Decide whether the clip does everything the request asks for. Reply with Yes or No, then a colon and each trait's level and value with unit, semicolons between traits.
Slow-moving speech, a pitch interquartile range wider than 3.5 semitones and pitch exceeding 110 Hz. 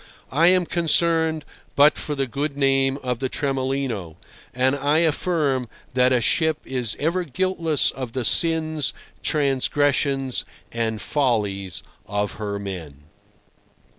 Yes: slow, 125 wpm; average, 4.4 semitones; low, 135 Hz